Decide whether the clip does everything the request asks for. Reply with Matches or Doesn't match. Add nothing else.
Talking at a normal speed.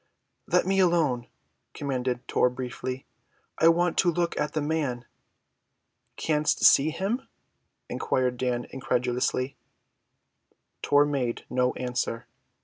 Doesn't match